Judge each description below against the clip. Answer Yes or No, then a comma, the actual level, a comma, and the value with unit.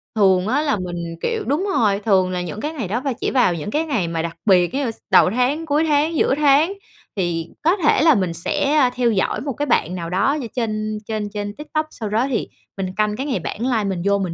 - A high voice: Yes, high, 220 Hz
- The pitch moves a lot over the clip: Yes, wide, 7.2 semitones